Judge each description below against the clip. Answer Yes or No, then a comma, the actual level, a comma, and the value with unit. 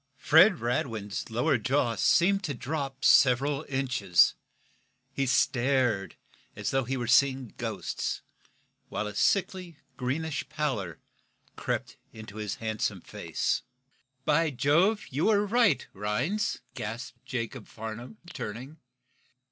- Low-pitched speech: Yes, low, 130 Hz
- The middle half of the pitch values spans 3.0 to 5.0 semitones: No, wide, 5.6 semitones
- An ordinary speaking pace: No, slow, 115 wpm